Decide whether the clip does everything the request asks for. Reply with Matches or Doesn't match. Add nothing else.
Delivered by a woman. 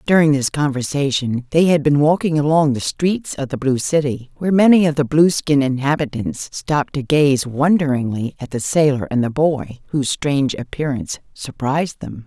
Matches